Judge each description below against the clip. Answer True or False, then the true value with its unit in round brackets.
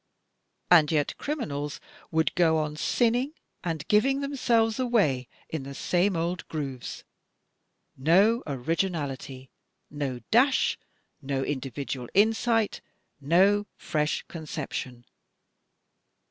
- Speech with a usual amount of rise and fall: False (7.5 semitones)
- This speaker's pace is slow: True (100 wpm)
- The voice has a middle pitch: True (160 Hz)